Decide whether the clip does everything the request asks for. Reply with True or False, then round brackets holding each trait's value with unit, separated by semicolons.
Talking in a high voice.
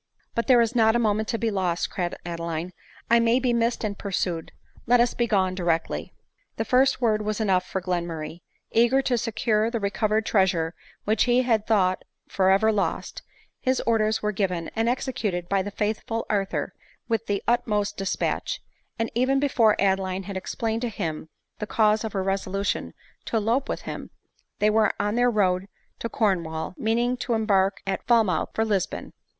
True (215 Hz)